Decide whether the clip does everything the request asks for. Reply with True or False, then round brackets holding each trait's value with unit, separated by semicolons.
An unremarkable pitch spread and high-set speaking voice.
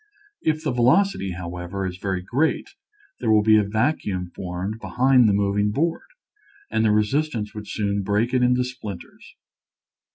False (4.2 semitones; 105 Hz)